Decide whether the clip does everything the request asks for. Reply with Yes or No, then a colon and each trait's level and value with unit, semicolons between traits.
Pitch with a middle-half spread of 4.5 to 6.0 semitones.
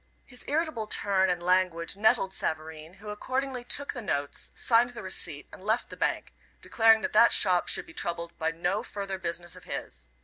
Yes: average, 4.9 semitones